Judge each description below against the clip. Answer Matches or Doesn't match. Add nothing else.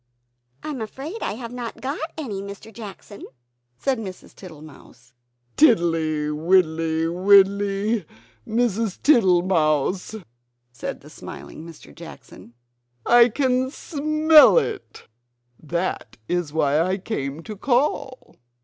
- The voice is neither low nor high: Doesn't match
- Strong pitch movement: Matches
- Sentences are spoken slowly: Matches